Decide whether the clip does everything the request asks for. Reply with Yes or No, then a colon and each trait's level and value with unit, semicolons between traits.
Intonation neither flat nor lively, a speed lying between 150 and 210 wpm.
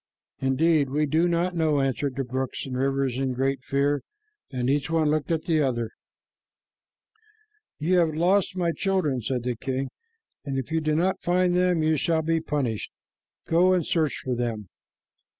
Yes: average, 3.9 semitones; average, 170 wpm